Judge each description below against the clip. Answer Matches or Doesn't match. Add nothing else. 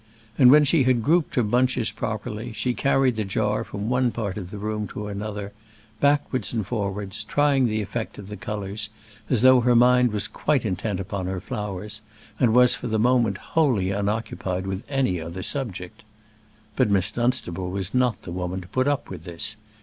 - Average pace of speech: Matches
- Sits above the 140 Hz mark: Doesn't match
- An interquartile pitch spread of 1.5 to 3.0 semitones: Doesn't match